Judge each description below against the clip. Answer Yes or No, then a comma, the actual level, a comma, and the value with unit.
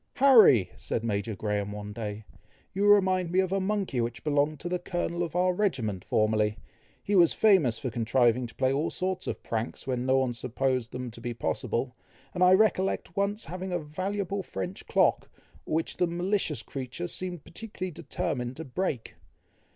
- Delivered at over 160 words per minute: Yes, average, 175 wpm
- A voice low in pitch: No, medium, 150 Hz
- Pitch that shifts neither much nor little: No, wide, 7.8 semitones